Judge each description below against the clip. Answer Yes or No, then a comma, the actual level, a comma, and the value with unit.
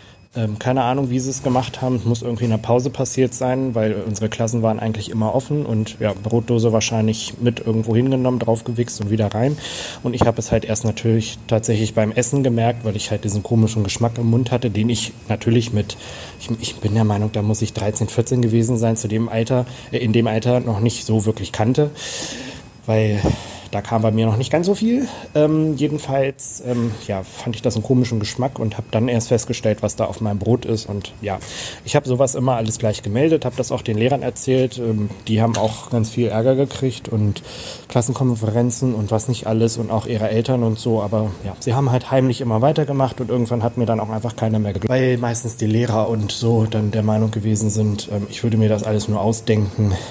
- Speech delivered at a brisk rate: Yes, fast, 220 wpm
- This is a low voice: Yes, low, 115 Hz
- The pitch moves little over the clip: Yes, narrow, 2.3 semitones